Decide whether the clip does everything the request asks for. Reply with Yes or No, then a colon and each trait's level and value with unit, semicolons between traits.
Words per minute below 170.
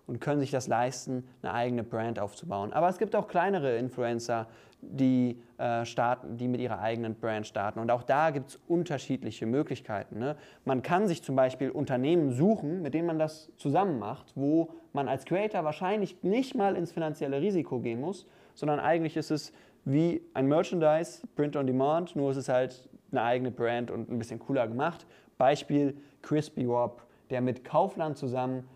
No: average, 175 wpm